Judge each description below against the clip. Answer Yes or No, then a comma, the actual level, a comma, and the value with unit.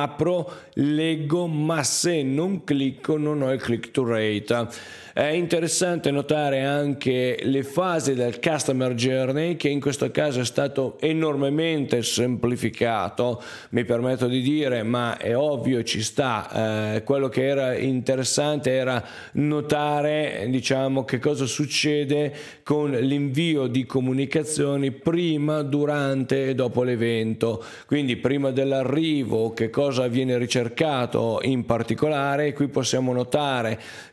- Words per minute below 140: Yes, average, 125 wpm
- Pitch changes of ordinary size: Yes, average, 3.1 semitones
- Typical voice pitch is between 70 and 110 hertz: No, low, 135 Hz